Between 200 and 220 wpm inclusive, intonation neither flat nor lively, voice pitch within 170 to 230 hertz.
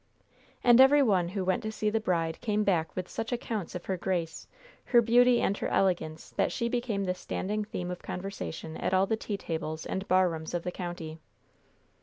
Yes: fast, 205 wpm; average, 3.9 semitones; high, 190 Hz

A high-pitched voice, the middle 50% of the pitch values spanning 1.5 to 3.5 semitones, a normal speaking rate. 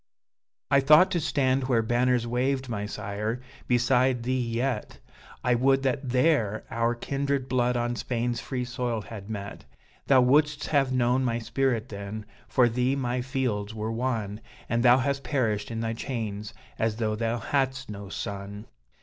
No: low, 120 Hz; average, 2.8 semitones; average, 160 wpm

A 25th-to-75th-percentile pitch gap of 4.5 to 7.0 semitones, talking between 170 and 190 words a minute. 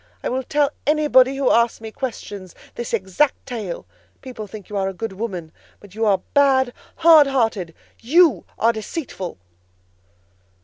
No: average, 5.2 semitones; average, 145 wpm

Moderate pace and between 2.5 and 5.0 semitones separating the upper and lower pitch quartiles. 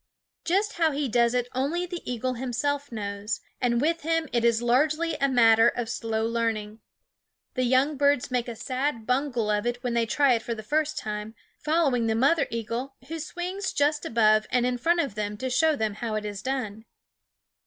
Yes: average, 195 wpm; average, 4.3 semitones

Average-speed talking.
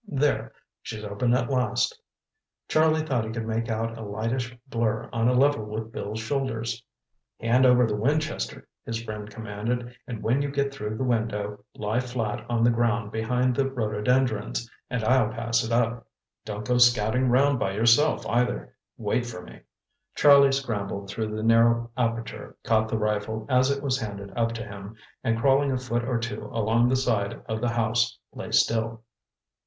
Yes: average, 175 wpm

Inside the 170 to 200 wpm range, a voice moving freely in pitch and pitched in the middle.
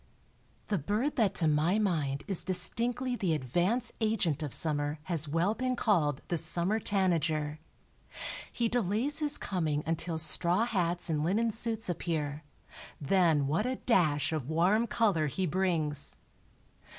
No: average, 140 wpm; wide, 5.8 semitones; medium, 175 Hz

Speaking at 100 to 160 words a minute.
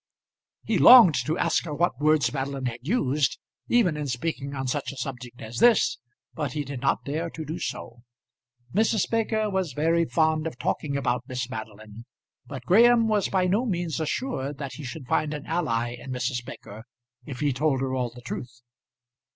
No: average, 185 wpm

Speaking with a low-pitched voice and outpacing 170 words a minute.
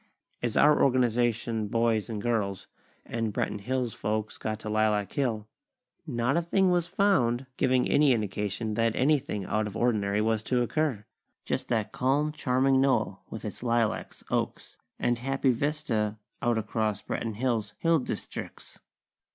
No: low, 120 Hz; average, 150 wpm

